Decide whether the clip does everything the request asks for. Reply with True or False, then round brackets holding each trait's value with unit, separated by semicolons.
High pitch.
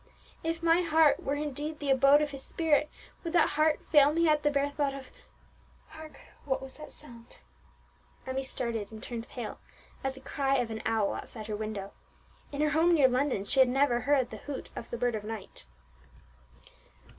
True (275 Hz)